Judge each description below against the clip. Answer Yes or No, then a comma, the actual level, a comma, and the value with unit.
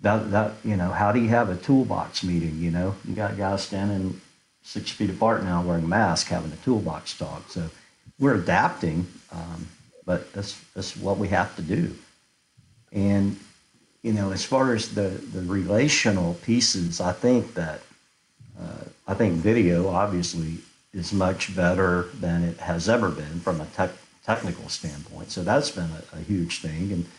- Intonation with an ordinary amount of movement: Yes, average, 3.3 semitones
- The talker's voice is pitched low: Yes, very low, 95 Hz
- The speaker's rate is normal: Yes, average, 175 wpm